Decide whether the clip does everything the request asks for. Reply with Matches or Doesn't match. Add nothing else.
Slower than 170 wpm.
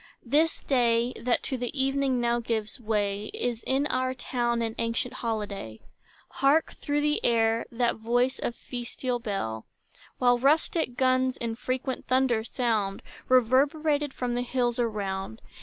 Matches